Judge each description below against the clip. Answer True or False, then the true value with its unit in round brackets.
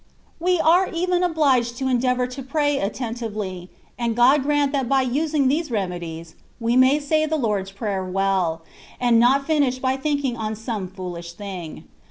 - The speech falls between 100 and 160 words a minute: False (175 wpm)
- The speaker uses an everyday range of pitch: False (6.4 semitones)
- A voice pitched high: True (250 Hz)